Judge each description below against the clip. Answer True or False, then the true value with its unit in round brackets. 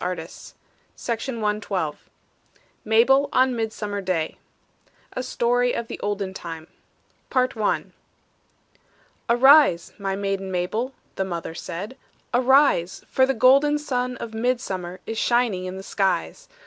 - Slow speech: True (115 wpm)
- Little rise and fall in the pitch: False (5.0 semitones)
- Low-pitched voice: False (220 Hz)